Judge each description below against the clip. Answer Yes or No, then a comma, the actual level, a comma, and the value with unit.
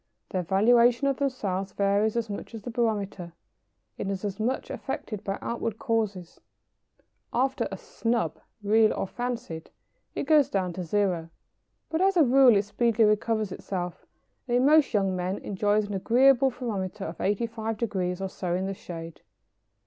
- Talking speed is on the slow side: No, average, 160 wpm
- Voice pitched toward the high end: Yes, high, 210 Hz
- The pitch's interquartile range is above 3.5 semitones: Yes, average, 3.9 semitones